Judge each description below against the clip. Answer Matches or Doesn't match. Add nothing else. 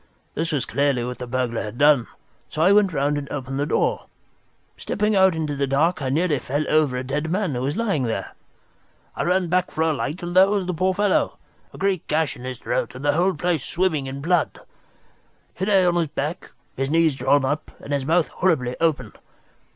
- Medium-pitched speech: Matches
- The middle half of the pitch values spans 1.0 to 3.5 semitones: Doesn't match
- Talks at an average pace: Doesn't match